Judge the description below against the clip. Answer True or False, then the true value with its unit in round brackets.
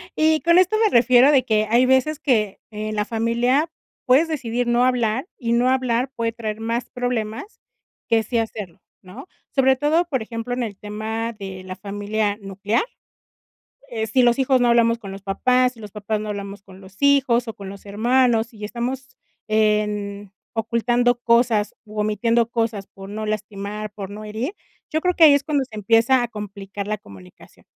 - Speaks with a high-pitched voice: True (230 Hz)